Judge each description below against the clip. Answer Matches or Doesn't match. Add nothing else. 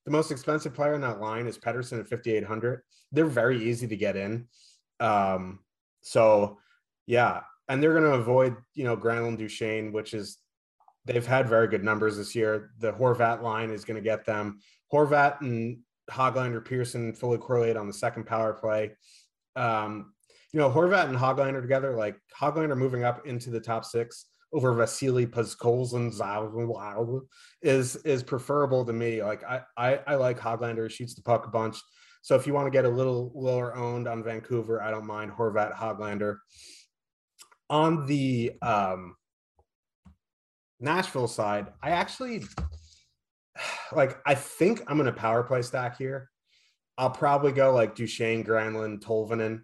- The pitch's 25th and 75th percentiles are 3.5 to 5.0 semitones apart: Doesn't match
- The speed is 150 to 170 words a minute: Matches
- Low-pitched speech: Matches